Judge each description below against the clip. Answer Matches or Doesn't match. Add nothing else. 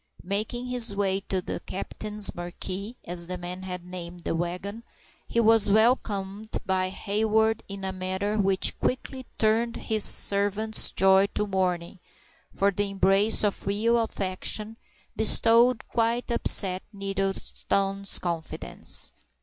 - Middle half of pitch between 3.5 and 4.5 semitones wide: Doesn't match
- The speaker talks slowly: Matches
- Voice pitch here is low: Doesn't match